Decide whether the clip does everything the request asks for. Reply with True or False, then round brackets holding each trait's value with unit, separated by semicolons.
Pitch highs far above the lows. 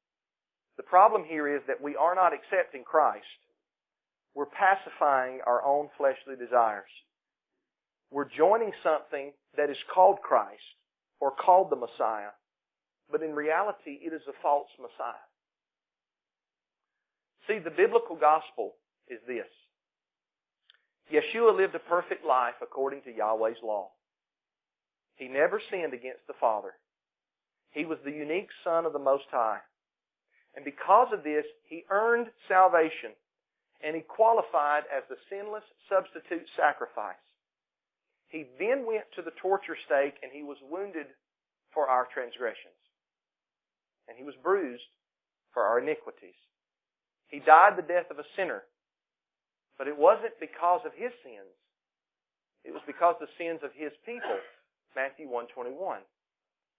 True (6.8 semitones)